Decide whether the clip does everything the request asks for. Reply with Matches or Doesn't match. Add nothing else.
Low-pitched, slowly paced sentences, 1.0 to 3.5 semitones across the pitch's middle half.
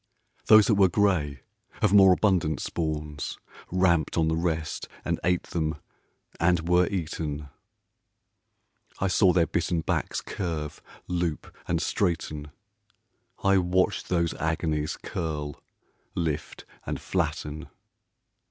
Matches